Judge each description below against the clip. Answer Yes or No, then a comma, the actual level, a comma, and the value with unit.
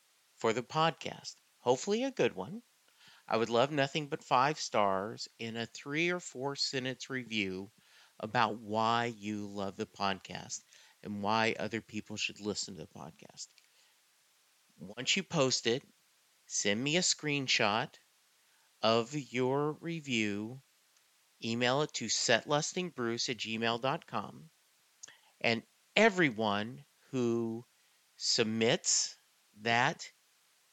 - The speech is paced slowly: Yes, slow, 115 wpm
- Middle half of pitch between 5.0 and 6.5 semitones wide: No, average, 4.6 semitones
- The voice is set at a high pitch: No, low, 120 Hz